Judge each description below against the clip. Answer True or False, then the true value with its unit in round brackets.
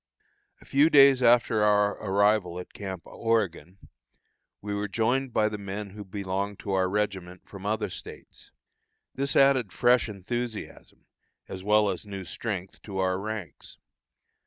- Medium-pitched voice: False (105 Hz)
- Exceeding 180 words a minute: False (145 wpm)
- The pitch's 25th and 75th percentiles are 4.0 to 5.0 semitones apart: False (2.8 semitones)